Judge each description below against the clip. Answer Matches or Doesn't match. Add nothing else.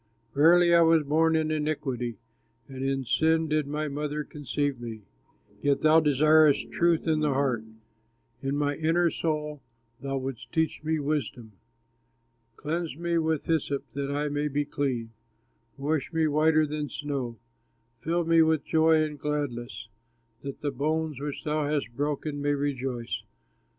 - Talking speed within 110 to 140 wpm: Doesn't match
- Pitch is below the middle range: Doesn't match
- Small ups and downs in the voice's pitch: Matches